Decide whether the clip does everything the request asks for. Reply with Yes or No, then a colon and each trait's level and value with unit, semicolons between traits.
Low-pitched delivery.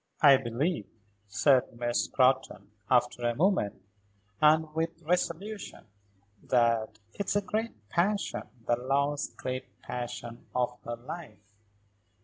Yes: low, 130 Hz